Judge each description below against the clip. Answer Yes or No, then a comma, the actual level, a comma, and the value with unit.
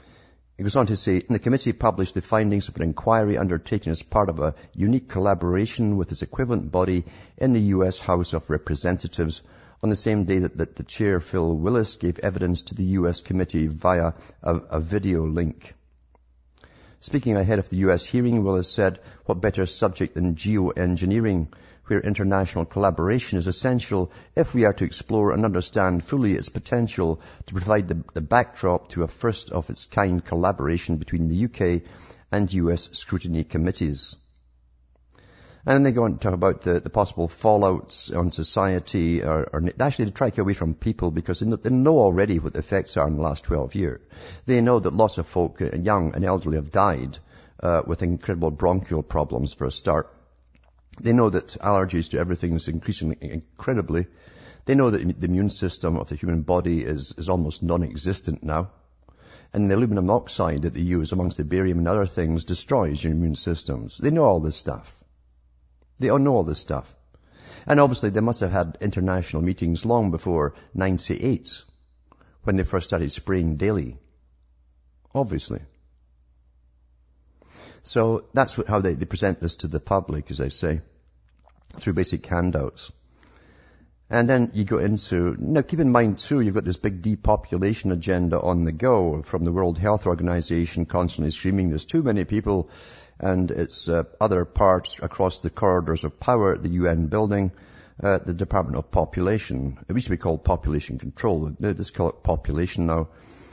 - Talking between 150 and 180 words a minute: Yes, average, 175 wpm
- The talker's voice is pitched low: Yes, very low, 90 Hz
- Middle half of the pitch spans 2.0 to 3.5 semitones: No, average, 4.0 semitones